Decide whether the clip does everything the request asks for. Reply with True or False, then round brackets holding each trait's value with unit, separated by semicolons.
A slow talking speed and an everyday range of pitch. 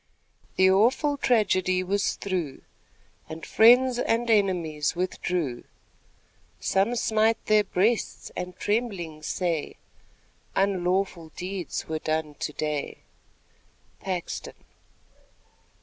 True (90 wpm; 4.5 semitones)